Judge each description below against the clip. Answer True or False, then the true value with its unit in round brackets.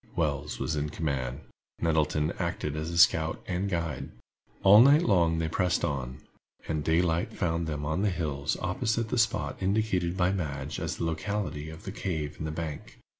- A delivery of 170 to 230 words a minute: True (175 wpm)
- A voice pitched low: True (80 Hz)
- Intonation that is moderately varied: True (3.5 semitones)